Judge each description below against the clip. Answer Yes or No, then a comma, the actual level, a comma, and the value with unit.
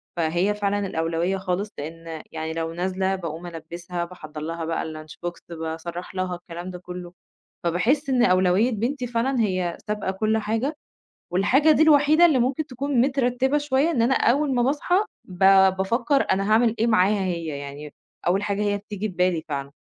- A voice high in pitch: Yes, high, 195 Hz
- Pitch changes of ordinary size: No, wide, 6.0 semitones